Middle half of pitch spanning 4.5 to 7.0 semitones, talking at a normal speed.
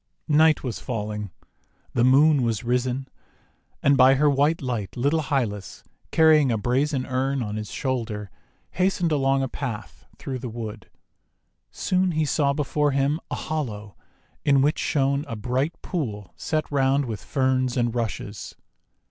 No: average, 3.7 semitones; average, 150 wpm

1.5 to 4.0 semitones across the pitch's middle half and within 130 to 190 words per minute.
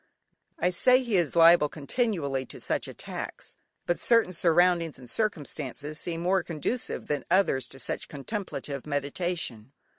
No: average, 4.5 semitones; average, 140 wpm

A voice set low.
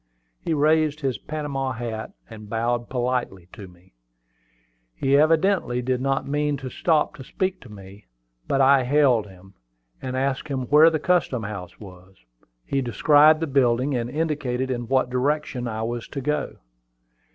Yes: low, 130 Hz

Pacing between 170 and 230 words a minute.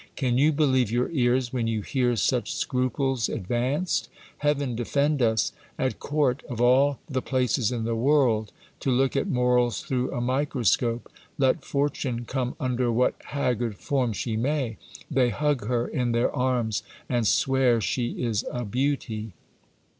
No: average, 155 wpm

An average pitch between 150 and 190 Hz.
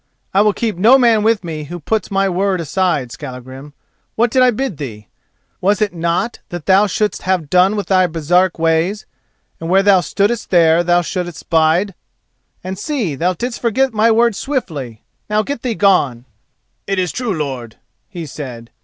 Yes: medium, 185 Hz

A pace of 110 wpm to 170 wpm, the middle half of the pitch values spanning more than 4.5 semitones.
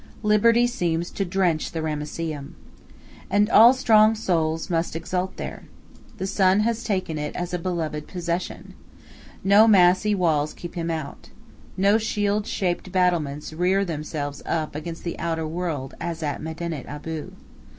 No: average, 145 wpm; average, 3.8 semitones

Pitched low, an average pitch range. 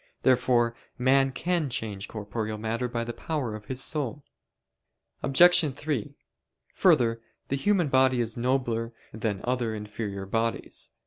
Yes: low, 120 Hz; average, 3.3 semitones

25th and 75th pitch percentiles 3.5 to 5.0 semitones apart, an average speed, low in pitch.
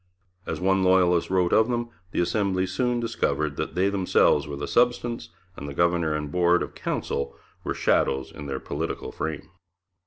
Yes: average, 4.5 semitones; average, 165 wpm; very low, 90 Hz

